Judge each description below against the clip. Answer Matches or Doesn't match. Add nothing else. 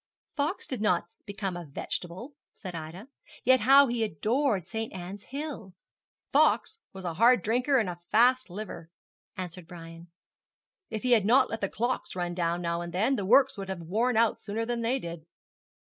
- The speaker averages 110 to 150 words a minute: Doesn't match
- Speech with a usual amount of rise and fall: Doesn't match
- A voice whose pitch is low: Doesn't match